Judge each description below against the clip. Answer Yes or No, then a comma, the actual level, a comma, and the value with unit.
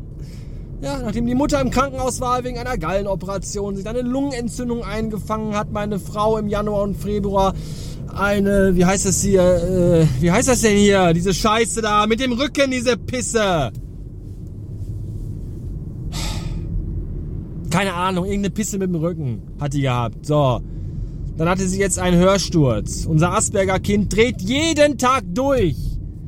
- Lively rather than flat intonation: Yes, wide, 5.8 semitones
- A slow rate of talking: No, average, 145 wpm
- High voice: Yes, high, 195 Hz